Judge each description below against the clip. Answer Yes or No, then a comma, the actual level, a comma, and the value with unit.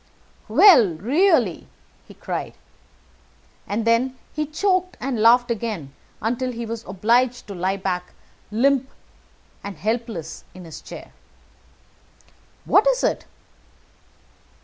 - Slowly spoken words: Yes, slow, 110 wpm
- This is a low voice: No, high, 230 Hz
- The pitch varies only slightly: No, average, 4.7 semitones